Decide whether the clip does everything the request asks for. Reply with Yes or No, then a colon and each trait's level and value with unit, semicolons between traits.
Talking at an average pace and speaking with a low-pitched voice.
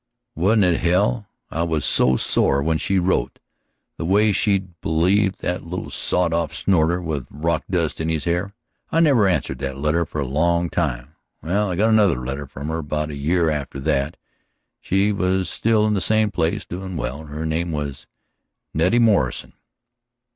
Yes: average, 175 wpm; very low, 85 Hz